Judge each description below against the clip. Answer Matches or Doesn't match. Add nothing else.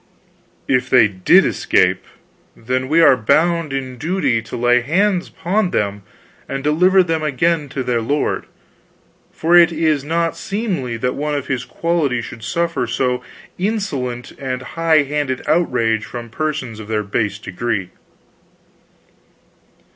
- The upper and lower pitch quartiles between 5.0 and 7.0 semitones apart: Matches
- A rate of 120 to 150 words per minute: Matches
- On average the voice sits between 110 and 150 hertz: Matches